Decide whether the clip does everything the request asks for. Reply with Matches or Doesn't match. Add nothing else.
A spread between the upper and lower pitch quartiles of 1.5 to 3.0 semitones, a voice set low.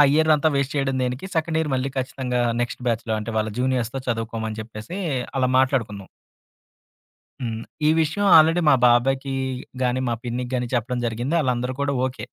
Matches